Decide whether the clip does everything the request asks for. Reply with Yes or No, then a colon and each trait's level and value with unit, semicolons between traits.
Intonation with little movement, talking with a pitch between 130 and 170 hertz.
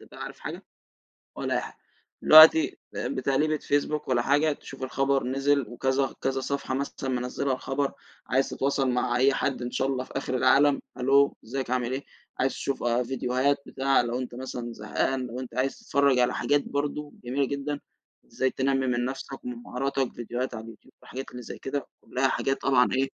Yes: narrow, 1.8 semitones; low, 135 Hz